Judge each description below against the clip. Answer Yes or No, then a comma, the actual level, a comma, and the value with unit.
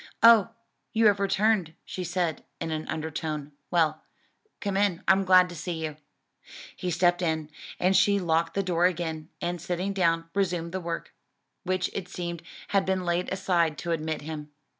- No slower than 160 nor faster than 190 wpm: Yes, average, 170 wpm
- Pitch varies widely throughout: No, average, 2.7 semitones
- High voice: No, medium, 175 Hz